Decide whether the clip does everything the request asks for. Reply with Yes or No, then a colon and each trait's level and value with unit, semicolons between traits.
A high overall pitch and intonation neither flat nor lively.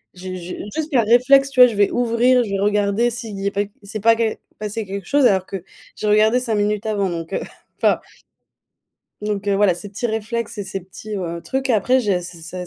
Yes: high, 210 Hz; average, 3.1 semitones